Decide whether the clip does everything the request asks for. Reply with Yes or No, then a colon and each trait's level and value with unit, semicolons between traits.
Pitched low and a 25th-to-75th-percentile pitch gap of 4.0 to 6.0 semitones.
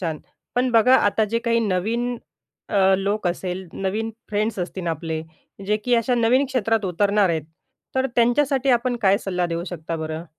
No: high, 210 Hz; average, 4.7 semitones